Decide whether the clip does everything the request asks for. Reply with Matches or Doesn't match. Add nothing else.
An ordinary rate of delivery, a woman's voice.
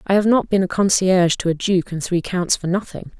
Doesn't match